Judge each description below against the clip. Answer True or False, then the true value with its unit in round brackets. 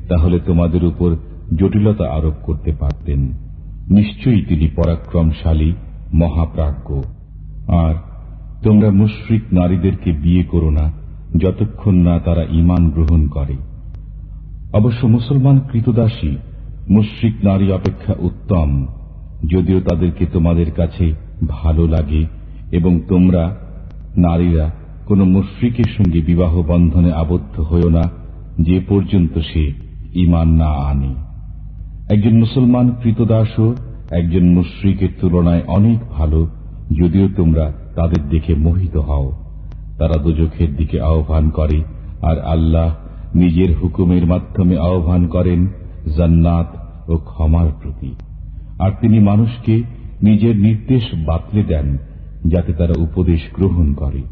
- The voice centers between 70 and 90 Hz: True (85 Hz)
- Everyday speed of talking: False (105 wpm)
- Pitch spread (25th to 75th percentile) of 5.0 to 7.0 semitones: False (3.1 semitones)